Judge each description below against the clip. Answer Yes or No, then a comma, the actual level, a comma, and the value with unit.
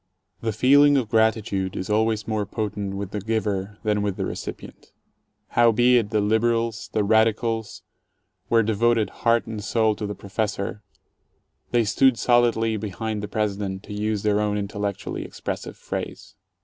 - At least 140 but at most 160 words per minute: Yes, average, 150 wpm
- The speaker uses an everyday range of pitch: No, narrow, 1.8 semitones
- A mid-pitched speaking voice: No, low, 110 Hz